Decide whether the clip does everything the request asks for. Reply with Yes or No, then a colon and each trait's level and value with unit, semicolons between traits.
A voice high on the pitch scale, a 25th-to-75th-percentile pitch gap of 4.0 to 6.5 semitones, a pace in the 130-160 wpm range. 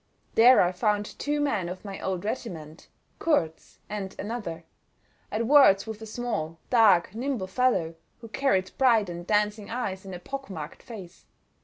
Yes: high, 210 Hz; average, 4.9 semitones; average, 150 wpm